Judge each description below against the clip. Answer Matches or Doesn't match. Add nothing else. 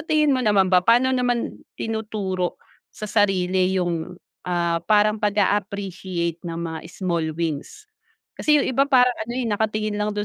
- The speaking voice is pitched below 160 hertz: Doesn't match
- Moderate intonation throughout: Matches